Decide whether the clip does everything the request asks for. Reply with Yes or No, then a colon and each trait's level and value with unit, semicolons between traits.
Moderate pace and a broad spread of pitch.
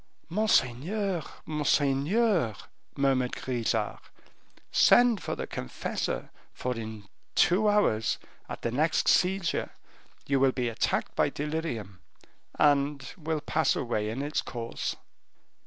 No: slow, 110 wpm; wide, 5.9 semitones